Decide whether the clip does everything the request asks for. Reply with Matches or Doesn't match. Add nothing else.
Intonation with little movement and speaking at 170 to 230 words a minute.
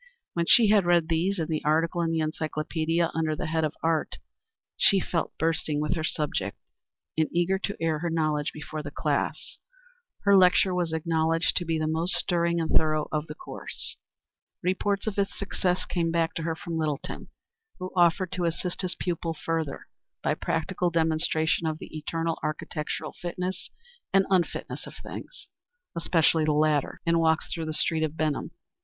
Matches